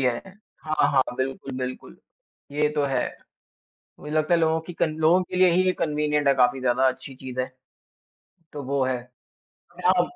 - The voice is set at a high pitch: No, medium, 145 Hz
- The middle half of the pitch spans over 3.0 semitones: Yes, average, 3.6 semitones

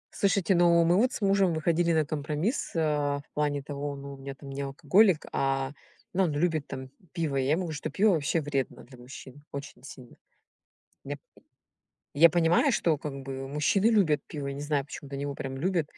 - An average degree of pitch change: Yes, average, 3.7 semitones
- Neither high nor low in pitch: Yes, medium, 150 Hz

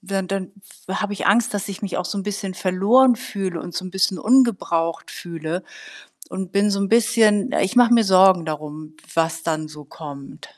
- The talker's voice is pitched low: No, high, 190 Hz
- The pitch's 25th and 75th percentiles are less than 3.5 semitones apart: No, average, 3.8 semitones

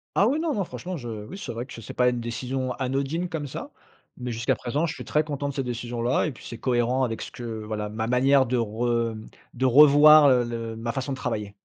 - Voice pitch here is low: Yes, low, 125 Hz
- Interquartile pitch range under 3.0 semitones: No, average, 3.3 semitones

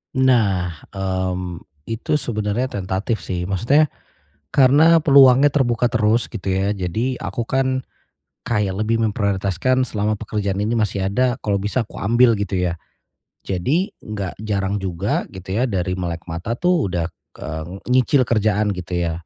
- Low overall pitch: Yes, low, 105 Hz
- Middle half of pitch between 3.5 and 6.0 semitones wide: Yes, average, 4.7 semitones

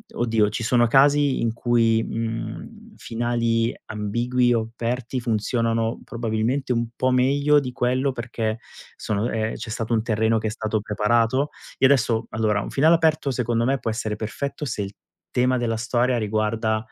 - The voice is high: No, low, 115 Hz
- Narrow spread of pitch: Yes, narrow, 2.3 semitones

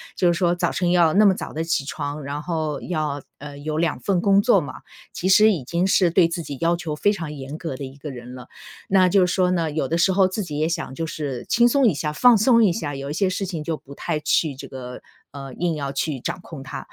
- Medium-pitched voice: Yes, medium, 165 Hz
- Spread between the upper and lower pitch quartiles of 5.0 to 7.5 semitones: No, average, 4.2 semitones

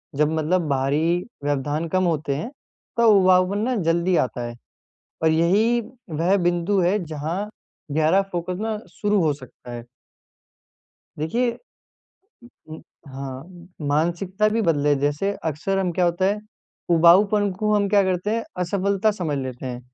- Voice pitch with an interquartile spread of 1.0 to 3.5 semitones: No, average, 4.8 semitones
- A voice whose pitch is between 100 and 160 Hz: No, medium, 175 Hz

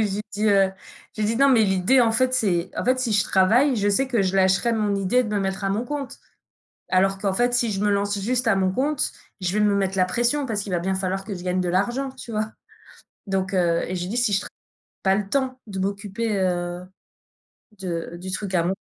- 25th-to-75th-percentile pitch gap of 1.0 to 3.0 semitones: No, average, 3.7 semitones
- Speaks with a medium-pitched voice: No, high, 200 Hz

